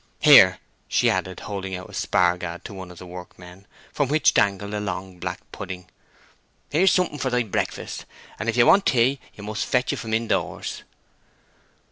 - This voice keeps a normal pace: Yes, average, 180 wpm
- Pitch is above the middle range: No, low, 100 Hz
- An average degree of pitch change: Yes, average, 4.6 semitones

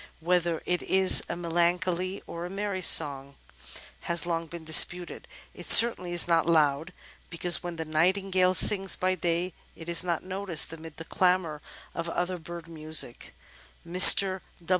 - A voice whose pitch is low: No, medium, 175 Hz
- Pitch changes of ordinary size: No, narrow, 2.1 semitones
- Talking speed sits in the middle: Yes, average, 150 wpm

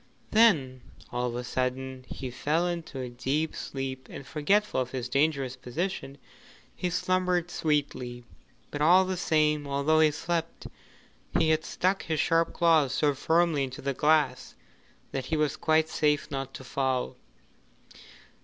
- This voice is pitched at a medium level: Yes, medium, 150 Hz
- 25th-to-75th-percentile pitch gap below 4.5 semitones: Yes, average, 3.9 semitones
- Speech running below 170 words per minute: Yes, average, 150 wpm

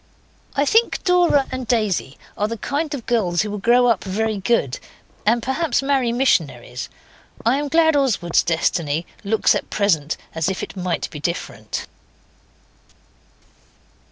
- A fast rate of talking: No, average, 145 wpm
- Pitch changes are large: Yes, wide, 7.5 semitones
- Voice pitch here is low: No, high, 220 Hz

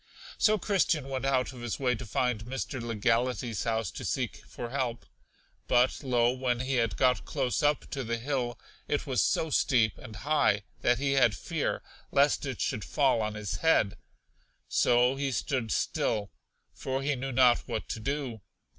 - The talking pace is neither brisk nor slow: Yes, average, 175 wpm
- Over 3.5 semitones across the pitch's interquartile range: No, average, 2.7 semitones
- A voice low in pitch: Yes, low, 125 Hz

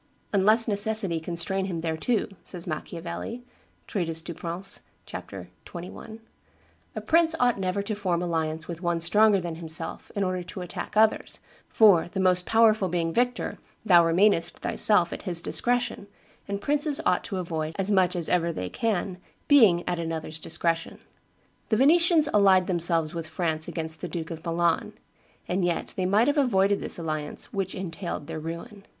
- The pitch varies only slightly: No, average, 3.7 semitones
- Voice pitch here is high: No, medium, 180 Hz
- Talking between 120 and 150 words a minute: No, average, 165 wpm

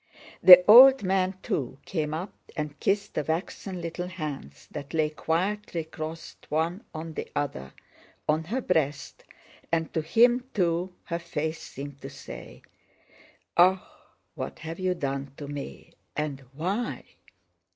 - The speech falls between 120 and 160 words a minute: Yes, average, 140 wpm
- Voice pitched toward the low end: No, medium, 160 Hz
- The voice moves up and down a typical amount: Yes, average, 3.7 semitones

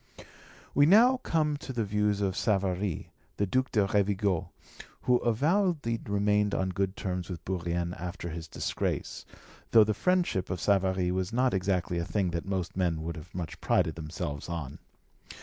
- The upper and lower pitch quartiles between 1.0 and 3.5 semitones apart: No, average, 3.9 semitones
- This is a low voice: Yes, very low, 95 Hz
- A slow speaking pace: No, average, 165 wpm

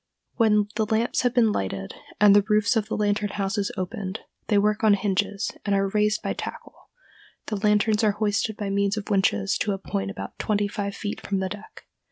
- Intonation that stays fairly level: Yes, narrow, 1.3 semitones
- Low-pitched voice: No, high, 205 Hz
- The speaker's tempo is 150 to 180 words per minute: No, average, 195 wpm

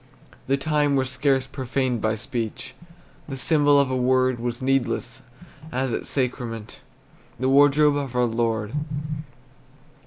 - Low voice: Yes, low, 130 Hz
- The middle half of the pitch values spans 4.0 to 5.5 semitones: No, narrow, 2.5 semitones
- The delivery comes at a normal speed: No, slow, 130 wpm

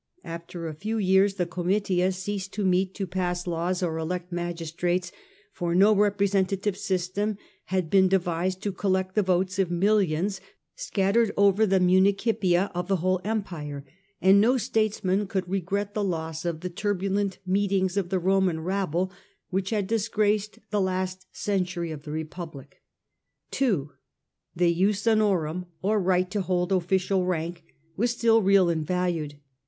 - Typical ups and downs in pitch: No, narrow, 2.3 semitones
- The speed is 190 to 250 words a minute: No, average, 160 wpm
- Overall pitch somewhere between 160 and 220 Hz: Yes, medium, 185 Hz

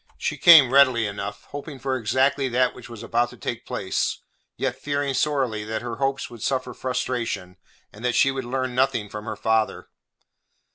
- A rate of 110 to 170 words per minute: No, average, 180 wpm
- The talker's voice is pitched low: Yes, low, 125 Hz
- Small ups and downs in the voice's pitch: No, average, 3.2 semitones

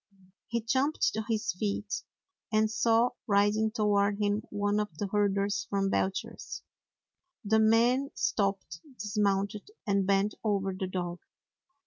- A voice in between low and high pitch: No, high, 205 Hz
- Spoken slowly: Yes, slow, 125 wpm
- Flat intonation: Yes, narrow, 1.7 semitones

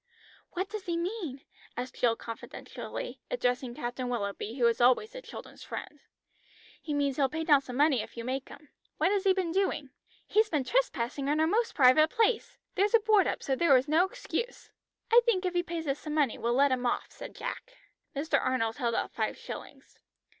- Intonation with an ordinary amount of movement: No, wide, 7.1 semitones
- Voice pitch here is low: No, very high, 295 Hz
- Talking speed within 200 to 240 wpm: Yes, fast, 205 wpm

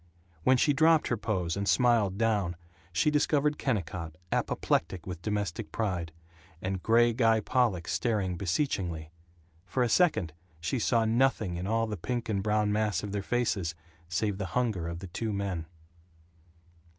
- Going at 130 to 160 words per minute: Yes, average, 155 wpm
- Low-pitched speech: Yes, low, 105 Hz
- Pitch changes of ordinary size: Yes, average, 4.8 semitones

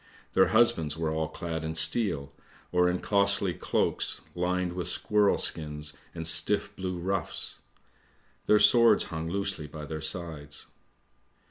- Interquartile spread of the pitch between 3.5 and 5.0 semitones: Yes, average, 3.8 semitones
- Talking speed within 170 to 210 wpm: No, slow, 135 wpm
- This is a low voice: Yes, very low, 85 Hz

